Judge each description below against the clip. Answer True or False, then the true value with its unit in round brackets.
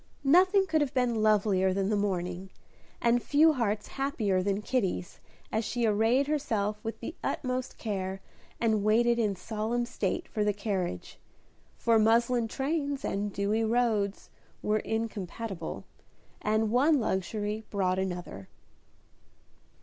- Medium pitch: False (215 Hz)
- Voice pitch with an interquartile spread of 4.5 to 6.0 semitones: False (3.3 semitones)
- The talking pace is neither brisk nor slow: False (130 wpm)